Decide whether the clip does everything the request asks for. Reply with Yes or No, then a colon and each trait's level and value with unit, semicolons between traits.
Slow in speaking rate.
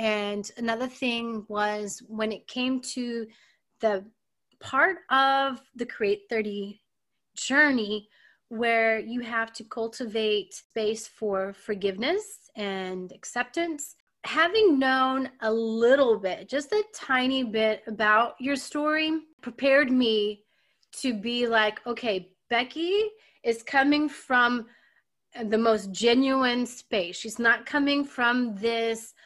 Yes: slow, 115 wpm